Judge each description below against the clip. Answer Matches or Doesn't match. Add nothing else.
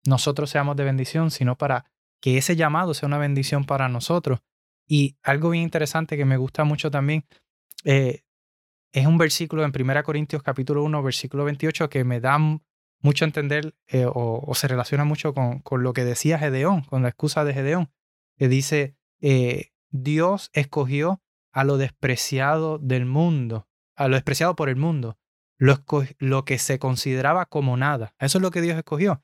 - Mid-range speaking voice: Matches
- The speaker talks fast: Doesn't match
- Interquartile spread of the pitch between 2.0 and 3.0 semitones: Matches